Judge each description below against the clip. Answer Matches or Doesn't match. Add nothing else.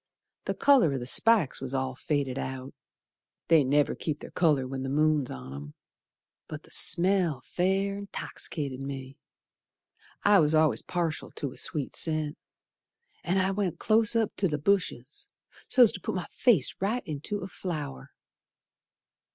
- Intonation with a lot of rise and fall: Matches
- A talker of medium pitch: Matches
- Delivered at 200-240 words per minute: Doesn't match